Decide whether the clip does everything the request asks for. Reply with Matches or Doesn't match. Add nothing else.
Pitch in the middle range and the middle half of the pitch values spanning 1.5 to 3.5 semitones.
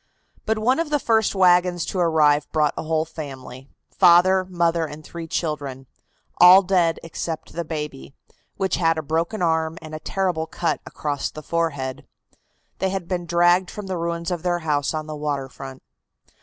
Matches